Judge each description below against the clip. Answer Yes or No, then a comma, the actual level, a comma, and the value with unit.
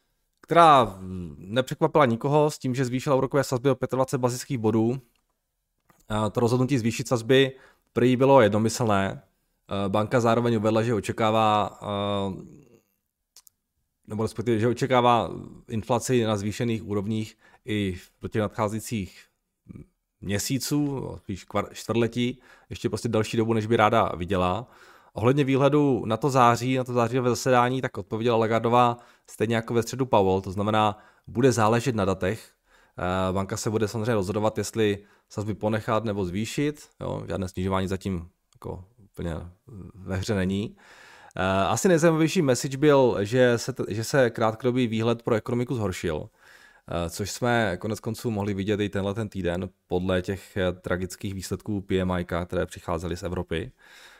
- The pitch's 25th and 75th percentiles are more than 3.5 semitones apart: Yes, average, 3.9 semitones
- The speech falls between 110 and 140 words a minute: Yes, average, 135 wpm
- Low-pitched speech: Yes, low, 110 Hz